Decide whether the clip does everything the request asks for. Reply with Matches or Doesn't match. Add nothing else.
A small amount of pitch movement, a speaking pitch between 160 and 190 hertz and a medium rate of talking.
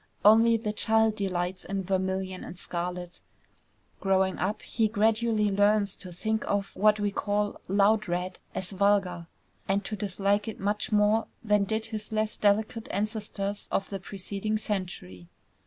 Doesn't match